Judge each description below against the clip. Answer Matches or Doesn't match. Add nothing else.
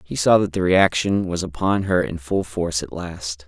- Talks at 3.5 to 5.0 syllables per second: Matches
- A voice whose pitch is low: Matches